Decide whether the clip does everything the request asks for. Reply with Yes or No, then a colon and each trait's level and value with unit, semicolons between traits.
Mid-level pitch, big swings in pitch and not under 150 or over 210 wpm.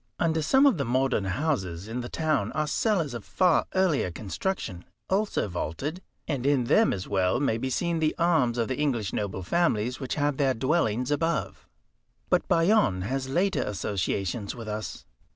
No: low, 130 Hz; wide, 7.3 semitones; average, 170 wpm